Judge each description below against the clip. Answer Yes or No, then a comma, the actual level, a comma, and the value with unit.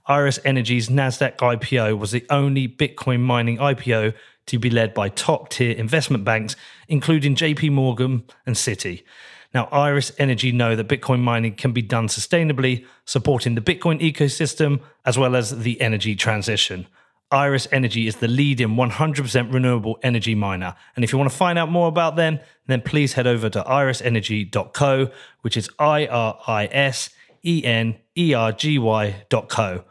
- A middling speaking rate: Yes, average, 160 wpm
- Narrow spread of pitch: No, average, 3.8 semitones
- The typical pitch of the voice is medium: No, low, 125 Hz